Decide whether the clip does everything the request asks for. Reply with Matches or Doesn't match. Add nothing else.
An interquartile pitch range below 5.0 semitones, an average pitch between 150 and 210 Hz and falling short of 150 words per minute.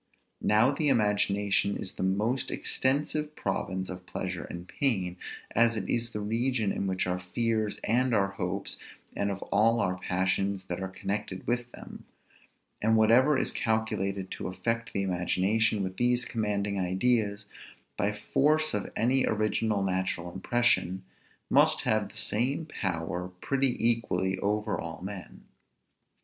Doesn't match